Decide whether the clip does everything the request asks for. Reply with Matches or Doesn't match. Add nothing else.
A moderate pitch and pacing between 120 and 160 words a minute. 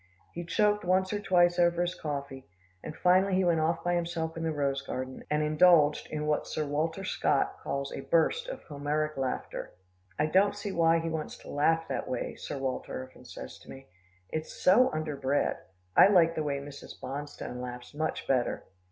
Doesn't match